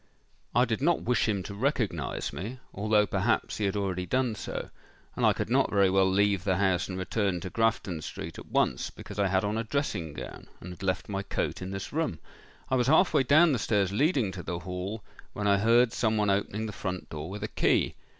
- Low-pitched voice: Yes, low, 100 Hz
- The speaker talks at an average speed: No, fast, 225 wpm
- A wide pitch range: No, average, 3.4 semitones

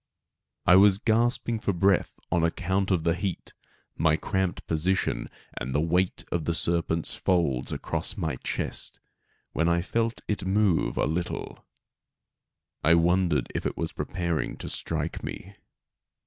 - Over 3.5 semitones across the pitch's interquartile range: No, narrow, 2.5 semitones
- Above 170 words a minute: No, average, 145 wpm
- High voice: No, very low, 90 Hz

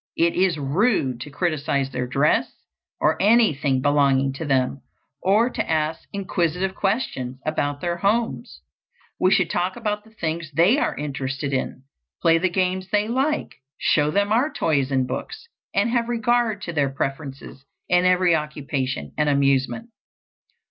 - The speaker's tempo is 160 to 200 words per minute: No, average, 150 wpm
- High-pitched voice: No, medium, 165 Hz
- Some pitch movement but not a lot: No, wide, 6.5 semitones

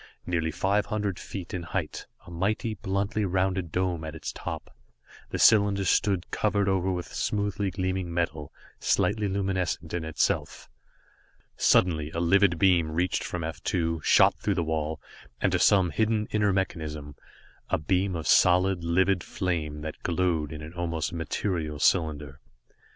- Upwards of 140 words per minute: Yes, average, 150 wpm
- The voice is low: Yes, very low, 90 Hz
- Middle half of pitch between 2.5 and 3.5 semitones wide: Yes, average, 3.1 semitones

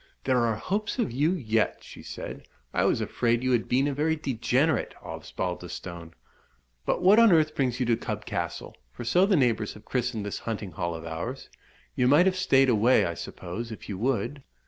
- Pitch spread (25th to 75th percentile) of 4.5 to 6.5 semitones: Yes, average, 5.1 semitones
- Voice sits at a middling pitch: No, low, 125 Hz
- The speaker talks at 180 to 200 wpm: Yes, average, 195 wpm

